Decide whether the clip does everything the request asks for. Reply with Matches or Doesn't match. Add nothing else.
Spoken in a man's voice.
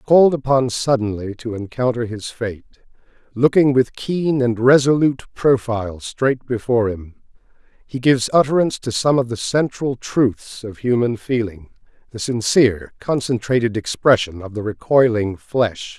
Matches